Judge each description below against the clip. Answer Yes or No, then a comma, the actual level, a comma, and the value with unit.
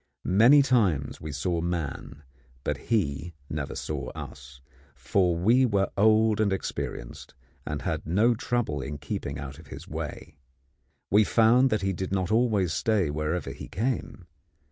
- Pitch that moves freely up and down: Yes, wide, 6.5 semitones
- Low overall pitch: Yes, very low, 95 Hz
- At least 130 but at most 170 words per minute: Yes, average, 150 wpm